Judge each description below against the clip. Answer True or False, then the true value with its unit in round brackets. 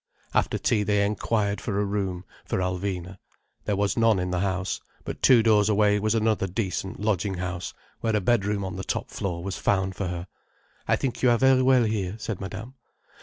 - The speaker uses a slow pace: False (200 wpm)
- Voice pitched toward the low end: True (100 Hz)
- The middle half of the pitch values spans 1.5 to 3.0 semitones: True (2.7 semitones)